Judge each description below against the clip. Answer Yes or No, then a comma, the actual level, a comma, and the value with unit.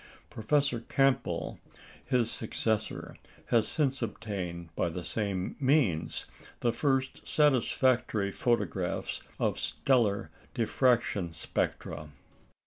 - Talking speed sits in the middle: No, slow, 90 wpm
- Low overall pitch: Yes, low, 115 Hz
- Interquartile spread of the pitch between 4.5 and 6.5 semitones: Yes, average, 4.8 semitones